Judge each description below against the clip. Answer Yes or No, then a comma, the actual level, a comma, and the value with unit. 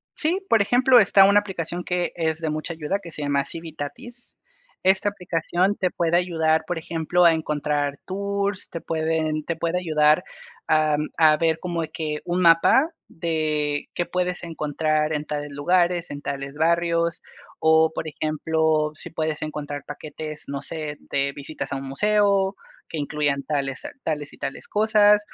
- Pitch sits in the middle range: Yes, medium, 160 Hz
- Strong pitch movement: No, average, 3.0 semitones